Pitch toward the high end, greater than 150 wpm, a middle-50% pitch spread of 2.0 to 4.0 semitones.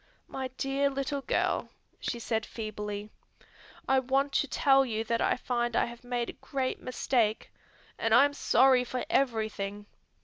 Yes: high, 245 Hz; average, 160 wpm; average, 3.3 semitones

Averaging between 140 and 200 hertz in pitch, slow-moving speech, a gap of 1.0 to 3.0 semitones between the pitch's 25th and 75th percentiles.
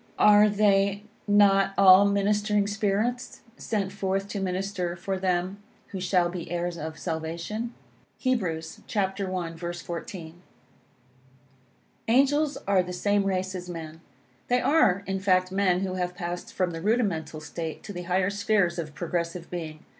No: high, 190 Hz; average, 145 wpm; average, 2.7 semitones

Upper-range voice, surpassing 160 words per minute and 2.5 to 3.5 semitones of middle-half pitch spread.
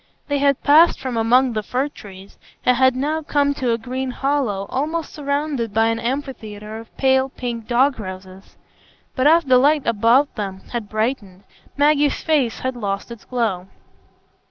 No: very high, 250 Hz; average, 170 wpm; average, 4.3 semitones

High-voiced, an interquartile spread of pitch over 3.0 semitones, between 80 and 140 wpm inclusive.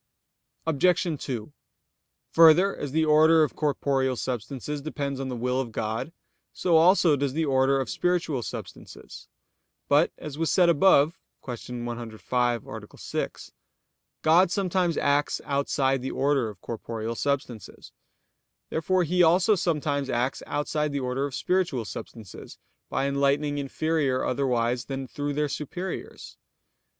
No: medium, 140 Hz; average, 3.8 semitones; slow, 135 wpm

